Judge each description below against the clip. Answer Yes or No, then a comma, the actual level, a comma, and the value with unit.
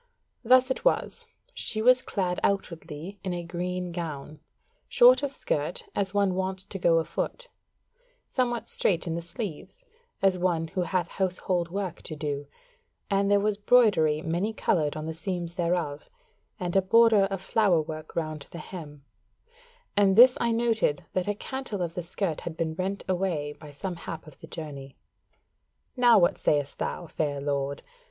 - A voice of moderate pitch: Yes, medium, 180 Hz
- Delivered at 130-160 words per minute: No, average, 170 wpm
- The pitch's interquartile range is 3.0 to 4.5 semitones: Yes, average, 4.1 semitones